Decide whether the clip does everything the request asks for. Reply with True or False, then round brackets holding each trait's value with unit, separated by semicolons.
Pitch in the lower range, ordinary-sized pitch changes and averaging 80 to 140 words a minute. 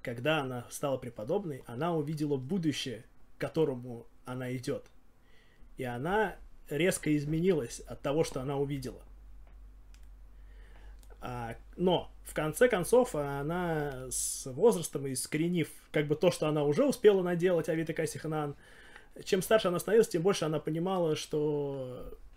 False (155 Hz; 4.2 semitones; 125 wpm)